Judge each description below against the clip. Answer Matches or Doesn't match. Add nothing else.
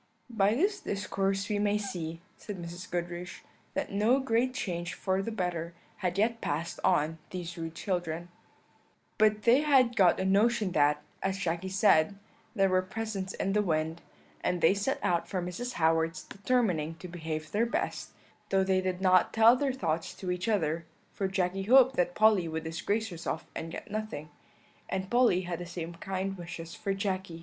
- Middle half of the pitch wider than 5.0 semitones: Doesn't match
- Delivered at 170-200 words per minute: Matches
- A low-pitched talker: Doesn't match